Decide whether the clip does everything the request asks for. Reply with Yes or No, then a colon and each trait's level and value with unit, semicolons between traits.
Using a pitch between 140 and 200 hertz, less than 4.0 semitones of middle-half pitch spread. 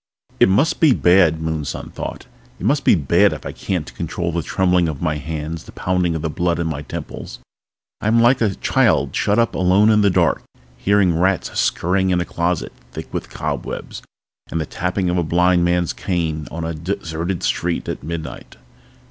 No: very low, 85 Hz; average, 2.7 semitones